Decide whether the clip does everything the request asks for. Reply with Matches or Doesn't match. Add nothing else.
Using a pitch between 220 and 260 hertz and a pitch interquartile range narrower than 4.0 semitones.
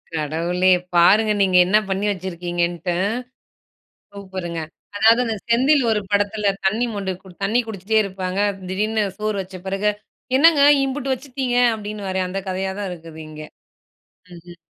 Doesn't match